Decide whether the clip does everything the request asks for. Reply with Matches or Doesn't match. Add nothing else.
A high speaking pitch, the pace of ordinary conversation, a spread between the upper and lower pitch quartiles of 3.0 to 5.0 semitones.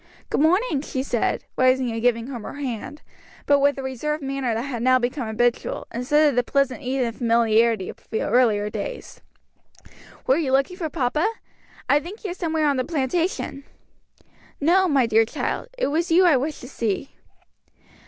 Matches